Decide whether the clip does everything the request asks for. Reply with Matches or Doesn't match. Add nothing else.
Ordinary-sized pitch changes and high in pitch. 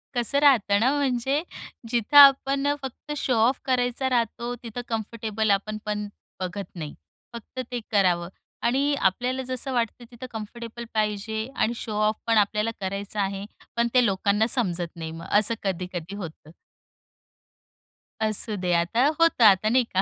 Matches